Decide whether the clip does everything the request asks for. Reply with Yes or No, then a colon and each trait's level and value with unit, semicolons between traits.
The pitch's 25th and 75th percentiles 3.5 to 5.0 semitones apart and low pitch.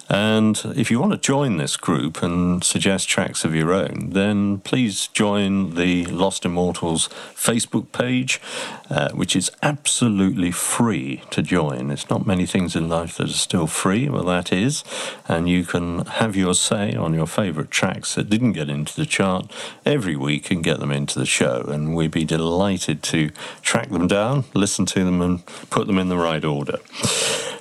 Yes: average, 3.8 semitones; very low, 90 Hz